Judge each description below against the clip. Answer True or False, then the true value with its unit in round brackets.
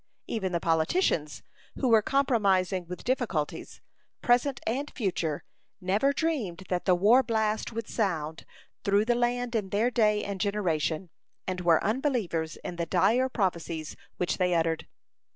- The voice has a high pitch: True (200 Hz)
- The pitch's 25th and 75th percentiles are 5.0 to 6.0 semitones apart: True (5.6 semitones)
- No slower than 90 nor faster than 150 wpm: True (145 wpm)